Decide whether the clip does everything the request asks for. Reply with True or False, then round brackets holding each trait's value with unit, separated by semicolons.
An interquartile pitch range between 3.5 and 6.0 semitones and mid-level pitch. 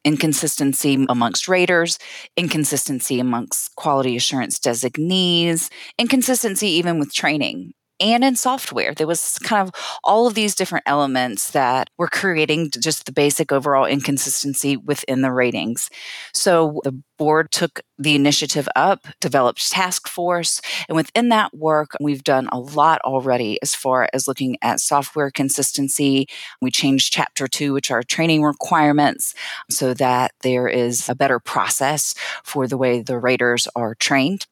True (3.8 semitones; 145 Hz)